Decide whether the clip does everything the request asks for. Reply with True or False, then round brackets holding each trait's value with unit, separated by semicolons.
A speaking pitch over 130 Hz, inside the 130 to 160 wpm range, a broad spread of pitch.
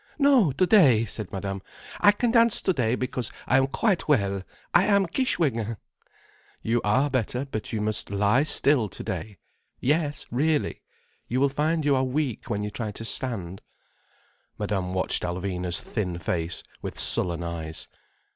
False (120 Hz; 145 wpm; 6.8 semitones)